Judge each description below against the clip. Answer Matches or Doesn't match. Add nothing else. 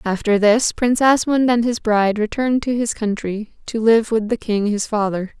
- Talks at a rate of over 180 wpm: Matches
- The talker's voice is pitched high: Matches